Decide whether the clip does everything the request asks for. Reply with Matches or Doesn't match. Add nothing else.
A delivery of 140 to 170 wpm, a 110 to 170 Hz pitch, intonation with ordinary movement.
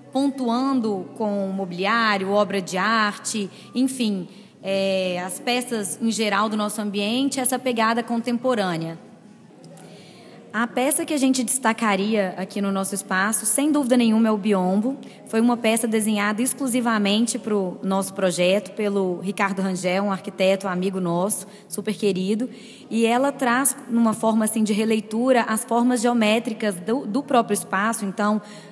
Doesn't match